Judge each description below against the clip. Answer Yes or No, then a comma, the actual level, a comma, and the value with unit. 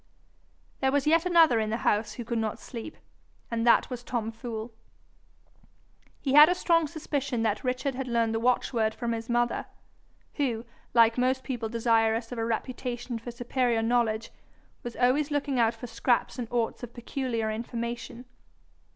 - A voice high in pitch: Yes, high, 240 Hz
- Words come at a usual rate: Yes, average, 165 wpm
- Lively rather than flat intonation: No, narrow, 2.4 semitones